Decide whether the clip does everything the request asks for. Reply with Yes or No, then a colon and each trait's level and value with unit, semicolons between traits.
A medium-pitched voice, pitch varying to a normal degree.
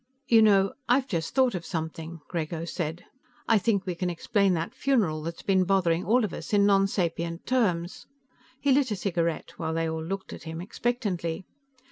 Yes: medium, 180 Hz; average, 3.9 semitones